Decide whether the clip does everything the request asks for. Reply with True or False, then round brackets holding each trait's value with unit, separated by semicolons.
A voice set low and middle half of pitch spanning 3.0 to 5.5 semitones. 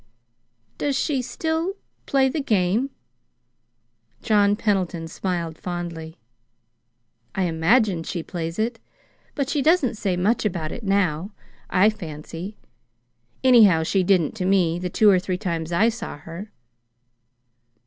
False (190 Hz; 4.9 semitones)